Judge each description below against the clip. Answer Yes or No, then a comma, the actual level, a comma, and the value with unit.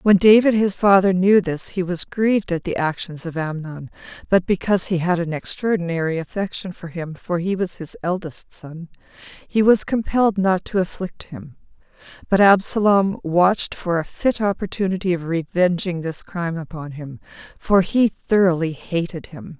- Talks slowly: No, average, 165 wpm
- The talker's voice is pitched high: No, medium, 180 Hz